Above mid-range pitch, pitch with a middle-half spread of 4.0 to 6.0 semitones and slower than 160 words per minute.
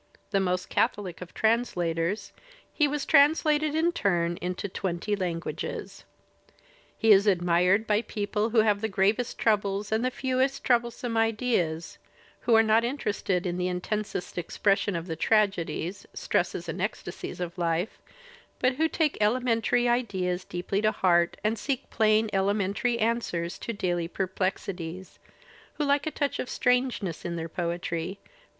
Yes: high, 205 Hz; average, 4.7 semitones; average, 150 wpm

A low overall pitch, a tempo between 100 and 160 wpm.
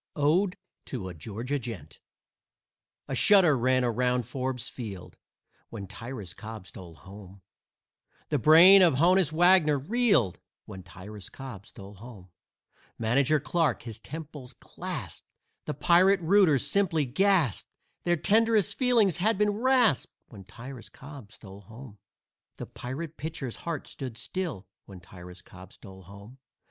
Yes: low, 130 Hz; slow, 135 wpm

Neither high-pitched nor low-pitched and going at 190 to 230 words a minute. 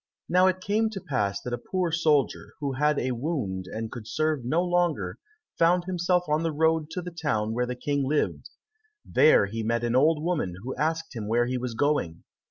Yes: medium, 145 Hz; fast, 205 wpm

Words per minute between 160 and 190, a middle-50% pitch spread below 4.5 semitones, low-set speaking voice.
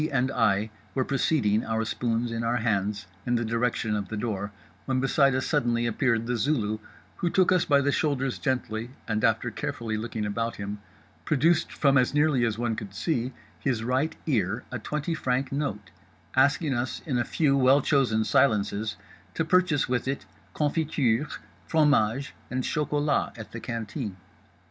Yes: average, 165 wpm; average, 4.1 semitones; low, 125 Hz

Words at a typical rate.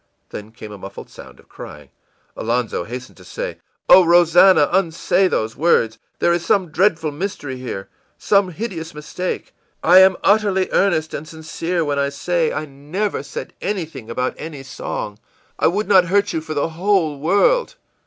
Yes: average, 170 wpm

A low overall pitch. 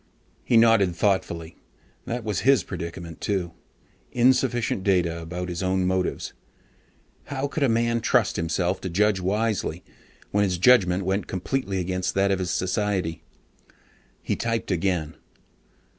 Yes: very low, 95 Hz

